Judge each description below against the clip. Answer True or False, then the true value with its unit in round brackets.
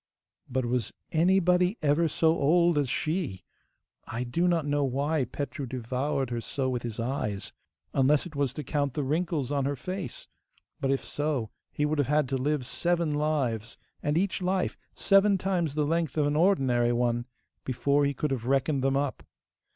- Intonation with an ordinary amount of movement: True (3.8 semitones)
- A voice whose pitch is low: False (145 Hz)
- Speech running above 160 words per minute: True (180 wpm)